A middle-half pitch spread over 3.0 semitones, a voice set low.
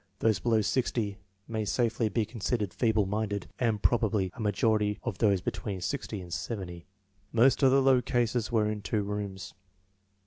No: average, 2.7 semitones; low, 110 Hz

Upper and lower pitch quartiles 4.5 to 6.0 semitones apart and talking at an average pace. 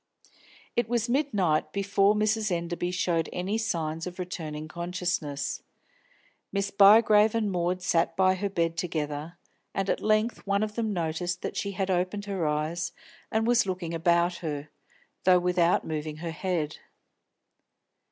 No: average, 3.4 semitones; average, 150 wpm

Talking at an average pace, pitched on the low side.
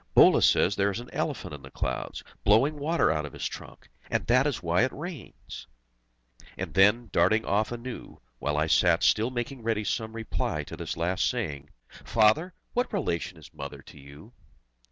Yes: average, 180 wpm; low, 110 Hz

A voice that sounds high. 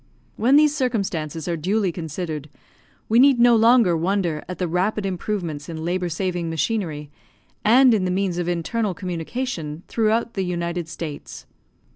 No: medium, 180 Hz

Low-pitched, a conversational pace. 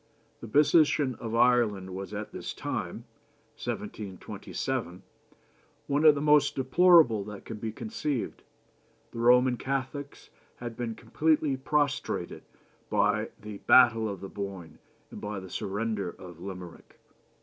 No: low, 115 Hz; slow, 125 wpm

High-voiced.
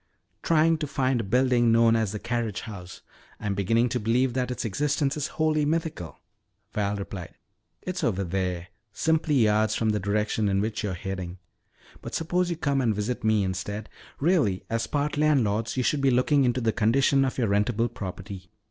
No: low, 115 Hz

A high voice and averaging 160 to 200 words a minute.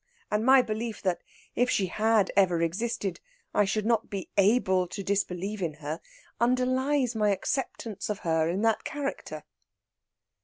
No: high, 210 Hz; average, 150 wpm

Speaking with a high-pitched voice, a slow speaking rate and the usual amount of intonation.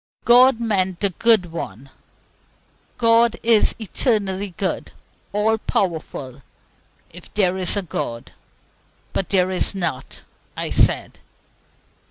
Yes: high, 195 Hz; slow, 110 wpm; average, 4.0 semitones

